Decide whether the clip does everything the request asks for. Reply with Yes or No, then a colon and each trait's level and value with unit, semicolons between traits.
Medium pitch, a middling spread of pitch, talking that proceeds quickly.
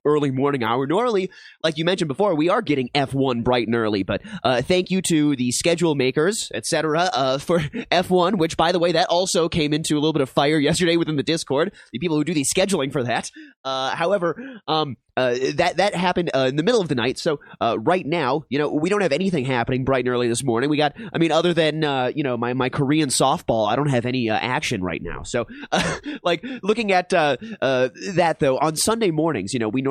Yes: medium, 150 Hz; average, 5.0 semitones; fast, 240 wpm